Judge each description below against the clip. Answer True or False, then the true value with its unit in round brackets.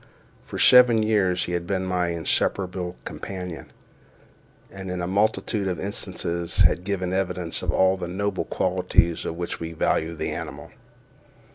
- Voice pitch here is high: False (90 Hz)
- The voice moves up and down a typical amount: False (1.8 semitones)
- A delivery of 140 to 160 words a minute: True (150 wpm)